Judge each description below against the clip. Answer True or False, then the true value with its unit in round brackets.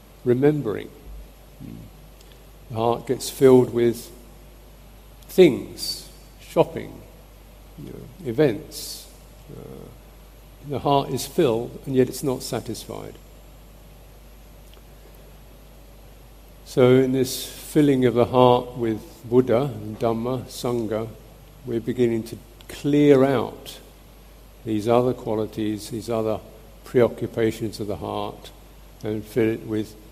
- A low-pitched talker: True (120 Hz)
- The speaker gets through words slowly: True (100 wpm)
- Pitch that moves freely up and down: False (2.7 semitones)